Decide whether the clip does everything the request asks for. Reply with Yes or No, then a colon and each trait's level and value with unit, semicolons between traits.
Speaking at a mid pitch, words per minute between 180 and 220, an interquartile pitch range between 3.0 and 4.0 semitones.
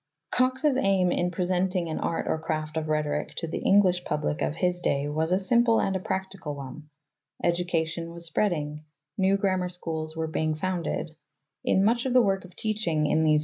Yes: medium, 175 Hz; fast, 205 wpm; average, 3.4 semitones